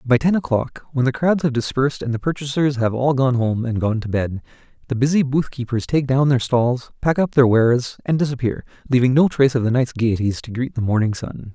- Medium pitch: No, low, 130 Hz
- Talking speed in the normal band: No, fast, 235 wpm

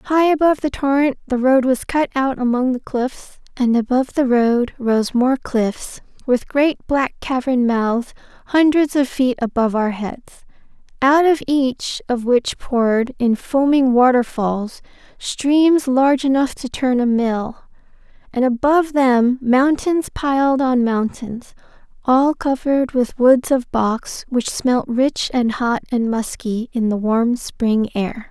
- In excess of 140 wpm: Yes, average, 150 wpm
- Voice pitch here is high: Yes, very high, 255 Hz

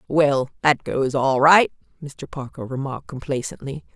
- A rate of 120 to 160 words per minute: Yes, slow, 135 wpm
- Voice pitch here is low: Yes, low, 130 Hz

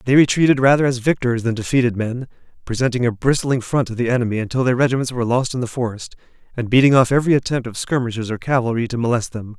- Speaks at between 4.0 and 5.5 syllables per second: No, 6.9 syllables/s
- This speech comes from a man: Yes, male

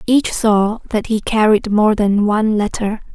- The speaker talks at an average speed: Yes, average, 170 wpm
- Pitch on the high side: Yes, high, 215 Hz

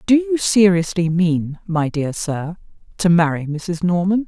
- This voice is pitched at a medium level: Yes, medium, 180 Hz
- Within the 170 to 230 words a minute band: No, average, 155 wpm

